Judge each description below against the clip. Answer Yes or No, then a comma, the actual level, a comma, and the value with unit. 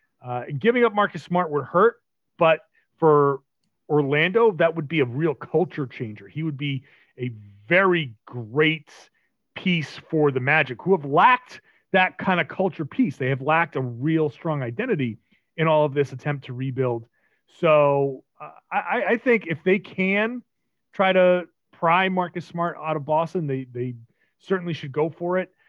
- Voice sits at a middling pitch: Yes, medium, 155 Hz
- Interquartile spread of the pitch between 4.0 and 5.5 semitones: Yes, average, 4.6 semitones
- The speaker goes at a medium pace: Yes, average, 170 wpm